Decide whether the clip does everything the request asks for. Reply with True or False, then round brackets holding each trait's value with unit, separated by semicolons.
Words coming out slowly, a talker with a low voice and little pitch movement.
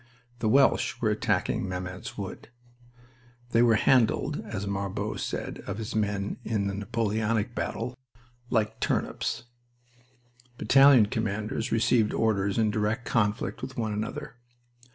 True (125 wpm; 110 Hz; 2.2 semitones)